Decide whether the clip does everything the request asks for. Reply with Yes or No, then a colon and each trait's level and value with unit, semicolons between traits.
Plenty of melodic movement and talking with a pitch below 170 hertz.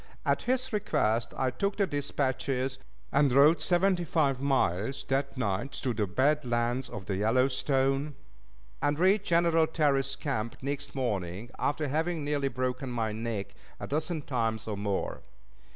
No: average, 4.2 semitones; low, 135 Hz